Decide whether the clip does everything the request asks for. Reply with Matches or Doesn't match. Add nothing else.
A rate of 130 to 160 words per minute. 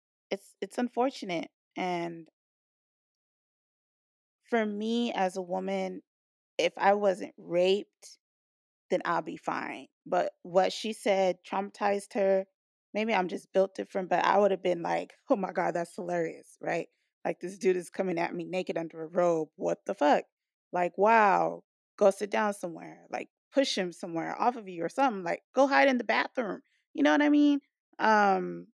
Doesn't match